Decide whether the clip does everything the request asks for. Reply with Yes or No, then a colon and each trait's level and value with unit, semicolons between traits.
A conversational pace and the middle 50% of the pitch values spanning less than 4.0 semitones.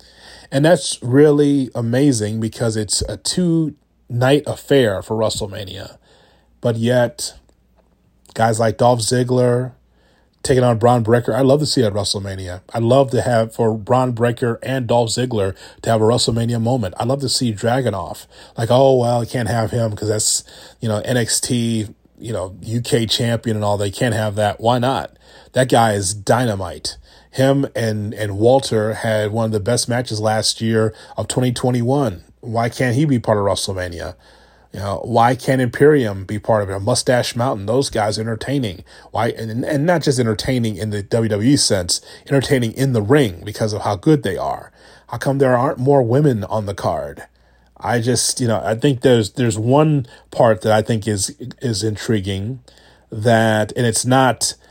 Yes: average, 180 wpm; average, 3.2 semitones